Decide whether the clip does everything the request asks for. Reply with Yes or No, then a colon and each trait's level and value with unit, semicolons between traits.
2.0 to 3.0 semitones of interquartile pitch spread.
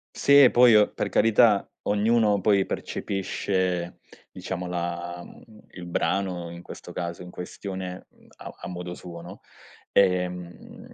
Yes: narrow, 2.6 semitones